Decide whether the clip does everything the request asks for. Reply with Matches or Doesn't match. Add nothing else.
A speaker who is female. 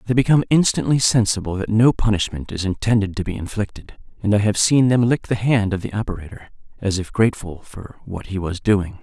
Doesn't match